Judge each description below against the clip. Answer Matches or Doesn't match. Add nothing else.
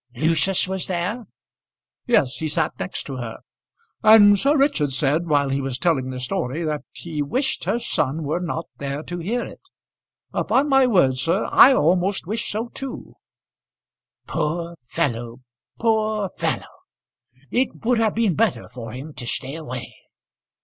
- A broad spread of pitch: Matches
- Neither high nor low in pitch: Matches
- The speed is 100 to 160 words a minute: Matches